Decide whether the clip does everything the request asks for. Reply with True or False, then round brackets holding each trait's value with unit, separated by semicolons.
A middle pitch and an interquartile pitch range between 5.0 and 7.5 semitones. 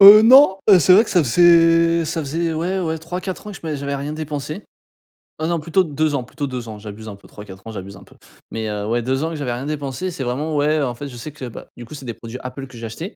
True (150 Hz; 5.3 semitones)